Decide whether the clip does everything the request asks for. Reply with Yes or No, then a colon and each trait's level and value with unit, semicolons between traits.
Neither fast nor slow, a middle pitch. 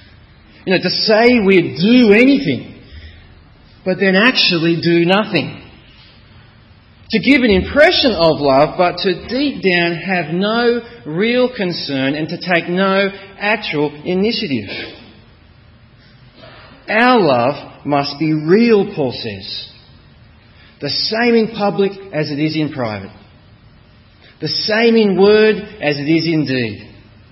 No: slow, 125 wpm; medium, 170 Hz